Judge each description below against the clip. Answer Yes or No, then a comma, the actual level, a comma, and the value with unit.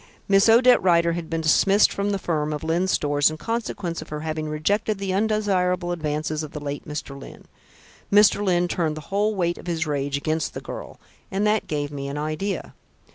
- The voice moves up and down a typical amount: Yes, average, 4.5 semitones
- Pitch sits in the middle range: Yes, medium, 170 Hz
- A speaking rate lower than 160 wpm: No, average, 200 wpm